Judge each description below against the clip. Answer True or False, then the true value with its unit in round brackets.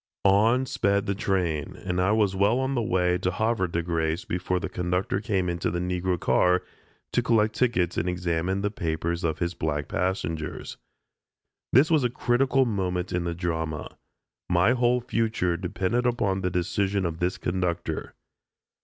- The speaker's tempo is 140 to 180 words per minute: True (165 wpm)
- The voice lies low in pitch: True (90 Hz)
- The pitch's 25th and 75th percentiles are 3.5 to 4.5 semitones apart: True (3.8 semitones)